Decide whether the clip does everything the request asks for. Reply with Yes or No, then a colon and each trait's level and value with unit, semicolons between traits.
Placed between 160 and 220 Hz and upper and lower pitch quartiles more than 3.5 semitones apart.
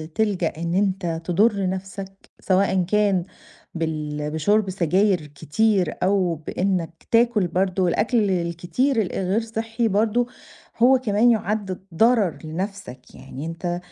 Yes: high, 190 Hz; average, 3.9 semitones